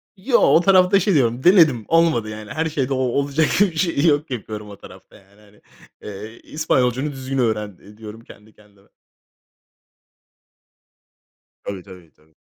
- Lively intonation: Yes, wide, 6.8 semitones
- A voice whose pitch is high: No, low, 125 Hz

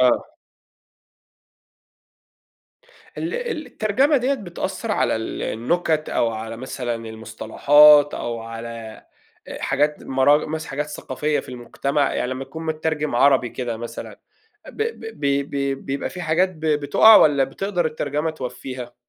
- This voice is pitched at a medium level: Yes, medium, 145 Hz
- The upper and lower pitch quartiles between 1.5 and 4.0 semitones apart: No, average, 4.4 semitones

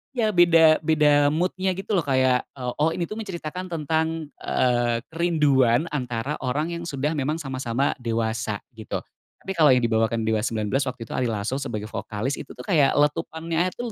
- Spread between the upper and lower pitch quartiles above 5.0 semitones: Yes, wide, 5.4 semitones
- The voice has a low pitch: No, medium, 145 Hz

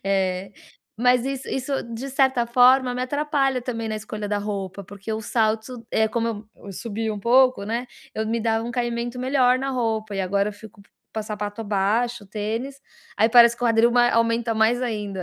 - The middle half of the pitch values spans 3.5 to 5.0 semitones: No, average, 2.8 semitones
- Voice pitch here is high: Yes, high, 230 Hz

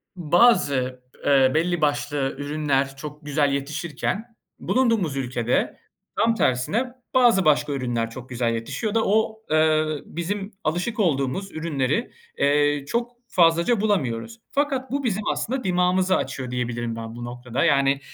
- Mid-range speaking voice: Yes, medium, 150 Hz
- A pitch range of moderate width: No, wide, 6.9 semitones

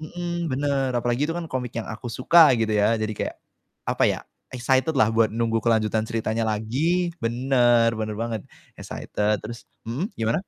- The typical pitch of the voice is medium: No, low, 120 Hz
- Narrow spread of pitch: No, average, 3.2 semitones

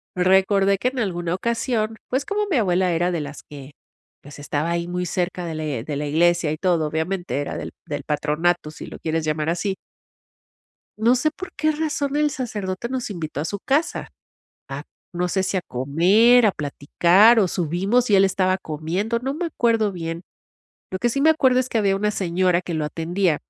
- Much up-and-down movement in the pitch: Yes, wide, 5.7 semitones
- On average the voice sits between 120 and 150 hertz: No, medium, 185 Hz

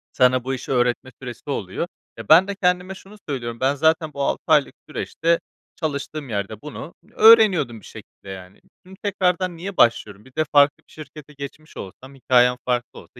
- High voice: No, medium, 140 Hz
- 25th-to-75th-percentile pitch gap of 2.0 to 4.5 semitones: No, wide, 5.5 semitones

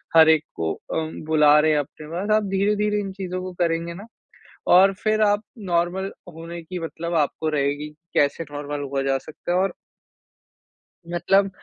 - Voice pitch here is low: No, medium, 170 Hz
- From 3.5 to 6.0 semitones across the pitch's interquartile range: Yes, average, 4.0 semitones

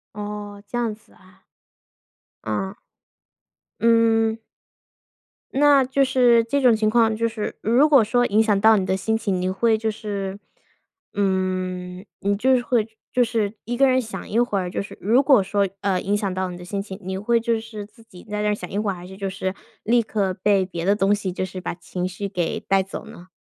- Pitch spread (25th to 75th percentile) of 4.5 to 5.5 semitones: No, average, 3.2 semitones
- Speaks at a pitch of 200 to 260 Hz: Yes, high, 210 Hz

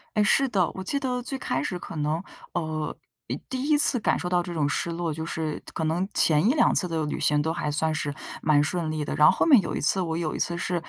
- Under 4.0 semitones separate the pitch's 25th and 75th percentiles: Yes, average, 3.5 semitones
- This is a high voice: No, medium, 170 Hz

